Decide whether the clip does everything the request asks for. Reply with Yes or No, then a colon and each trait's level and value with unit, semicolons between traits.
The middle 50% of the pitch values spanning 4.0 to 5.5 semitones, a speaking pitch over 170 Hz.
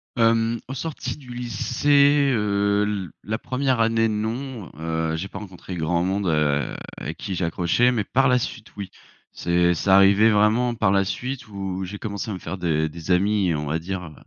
No: average, 4.6 semitones; low, 100 Hz